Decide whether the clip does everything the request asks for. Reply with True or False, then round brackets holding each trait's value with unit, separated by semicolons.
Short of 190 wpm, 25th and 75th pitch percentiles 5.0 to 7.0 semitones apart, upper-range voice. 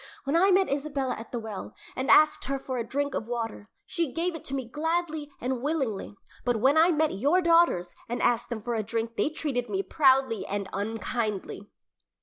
False (200 wpm; 5.4 semitones; 265 Hz)